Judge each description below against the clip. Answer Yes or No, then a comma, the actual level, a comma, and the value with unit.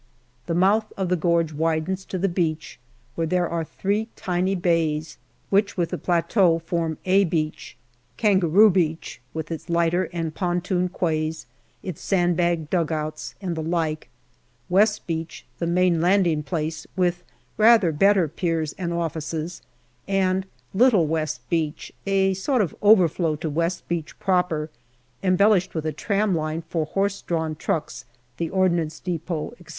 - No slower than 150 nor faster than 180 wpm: Yes, average, 155 wpm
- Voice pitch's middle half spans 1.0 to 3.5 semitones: Yes, average, 2.8 semitones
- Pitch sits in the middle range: Yes, medium, 170 Hz